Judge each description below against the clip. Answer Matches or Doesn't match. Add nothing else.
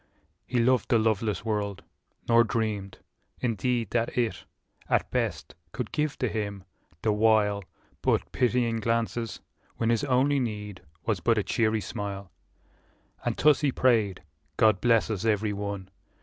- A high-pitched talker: Doesn't match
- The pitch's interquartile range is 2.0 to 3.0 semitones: Matches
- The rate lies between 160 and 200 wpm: Doesn't match